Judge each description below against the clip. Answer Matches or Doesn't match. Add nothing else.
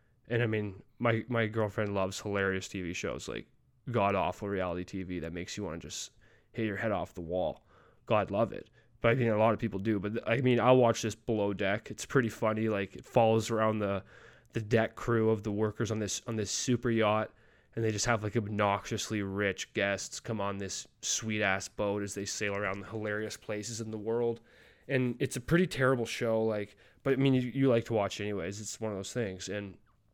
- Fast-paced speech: Matches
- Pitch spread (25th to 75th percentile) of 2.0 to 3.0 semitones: Matches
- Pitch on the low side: Matches